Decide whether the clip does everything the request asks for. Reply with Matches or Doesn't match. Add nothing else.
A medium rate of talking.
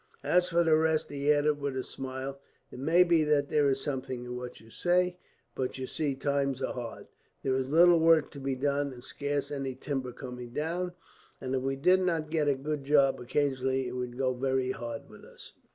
Doesn't match